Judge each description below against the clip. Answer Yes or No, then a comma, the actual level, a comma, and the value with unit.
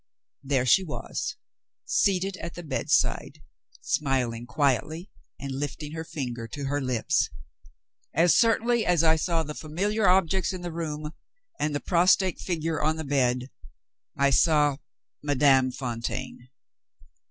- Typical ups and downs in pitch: Yes, average, 4.2 semitones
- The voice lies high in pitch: No, medium, 150 Hz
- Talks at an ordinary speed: No, slow, 130 wpm